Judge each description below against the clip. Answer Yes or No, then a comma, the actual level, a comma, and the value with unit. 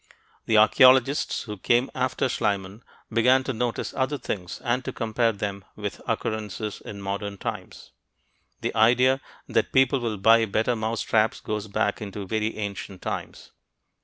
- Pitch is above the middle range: No, low, 110 Hz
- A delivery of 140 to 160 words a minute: Yes, average, 145 wpm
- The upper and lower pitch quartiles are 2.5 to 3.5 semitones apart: Yes, average, 3.1 semitones